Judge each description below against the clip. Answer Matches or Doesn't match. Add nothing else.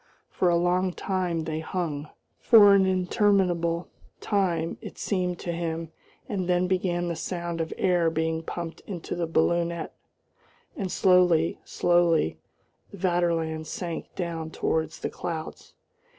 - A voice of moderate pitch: Matches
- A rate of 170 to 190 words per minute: Doesn't match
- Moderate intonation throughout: Doesn't match